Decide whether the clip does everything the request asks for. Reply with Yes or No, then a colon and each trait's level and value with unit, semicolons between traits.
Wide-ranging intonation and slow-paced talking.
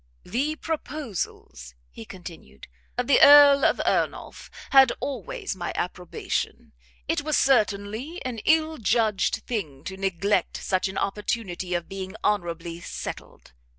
Yes: wide, 7.4 semitones; slow, 125 wpm